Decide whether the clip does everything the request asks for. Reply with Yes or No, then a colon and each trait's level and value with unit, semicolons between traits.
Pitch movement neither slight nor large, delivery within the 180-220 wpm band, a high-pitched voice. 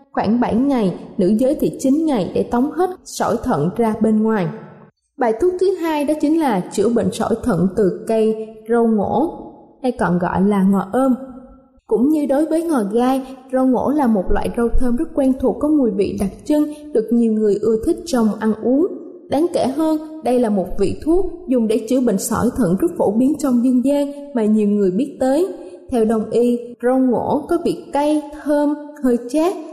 Yes: average, 4.9 semitones; average, 205 wpm; very high, 250 Hz